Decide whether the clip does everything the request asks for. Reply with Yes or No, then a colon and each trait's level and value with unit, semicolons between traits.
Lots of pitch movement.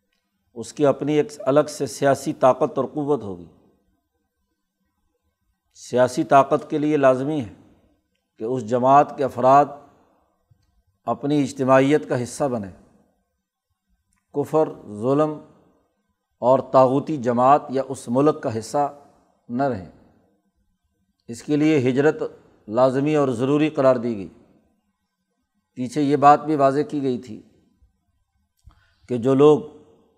Yes: wide, 6.0 semitones